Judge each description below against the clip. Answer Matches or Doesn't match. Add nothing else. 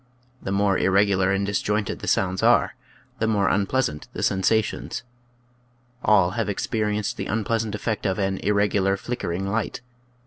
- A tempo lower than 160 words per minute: Matches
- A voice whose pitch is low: Matches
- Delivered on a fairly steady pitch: Matches